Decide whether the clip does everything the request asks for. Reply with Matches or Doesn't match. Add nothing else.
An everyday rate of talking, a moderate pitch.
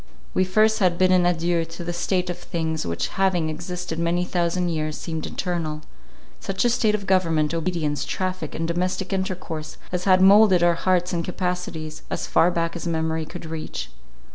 Matches